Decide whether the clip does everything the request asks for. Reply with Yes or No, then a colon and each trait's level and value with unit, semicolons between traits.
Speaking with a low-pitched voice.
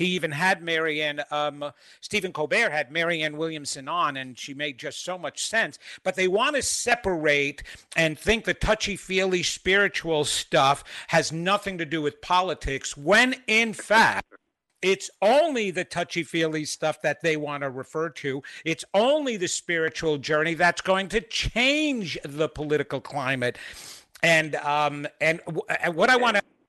No: medium, 165 Hz